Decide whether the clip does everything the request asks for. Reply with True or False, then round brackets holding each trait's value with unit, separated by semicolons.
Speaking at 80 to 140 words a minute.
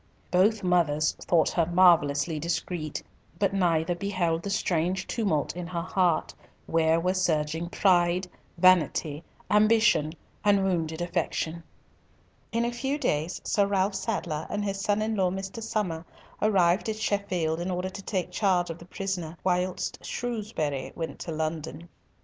False (150 wpm)